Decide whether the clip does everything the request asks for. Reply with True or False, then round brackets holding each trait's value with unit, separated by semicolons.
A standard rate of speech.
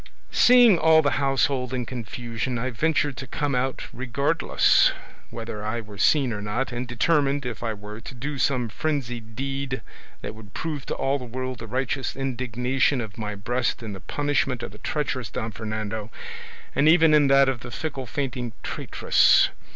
True (175 wpm)